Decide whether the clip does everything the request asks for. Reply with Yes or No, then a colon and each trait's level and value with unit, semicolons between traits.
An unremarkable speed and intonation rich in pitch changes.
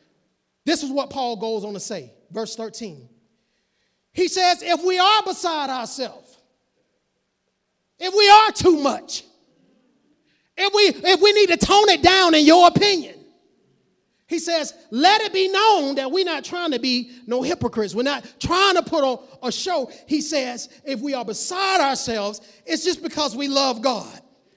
Yes: average, 170 wpm; wide, 6.6 semitones